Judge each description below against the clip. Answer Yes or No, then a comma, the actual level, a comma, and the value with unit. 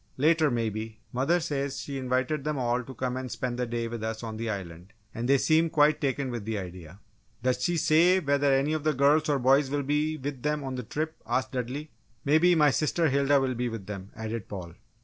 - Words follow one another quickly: Yes, fast, 225 wpm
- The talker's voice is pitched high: No, low, 130 Hz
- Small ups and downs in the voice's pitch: No, average, 4.2 semitones